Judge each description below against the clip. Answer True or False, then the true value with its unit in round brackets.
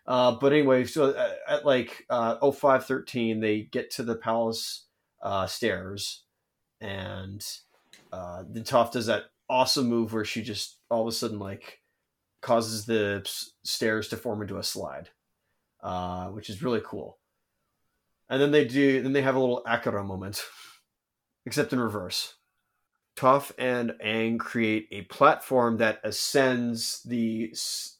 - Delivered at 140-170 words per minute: True (155 wpm)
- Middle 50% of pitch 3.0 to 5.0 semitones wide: True (3.3 semitones)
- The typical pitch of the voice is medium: False (115 Hz)